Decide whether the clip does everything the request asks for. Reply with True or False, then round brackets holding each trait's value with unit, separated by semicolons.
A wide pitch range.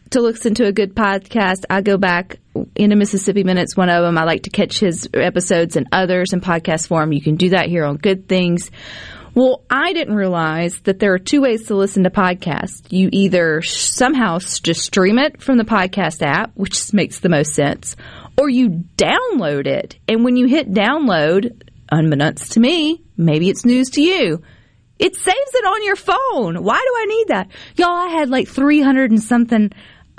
True (6.4 semitones)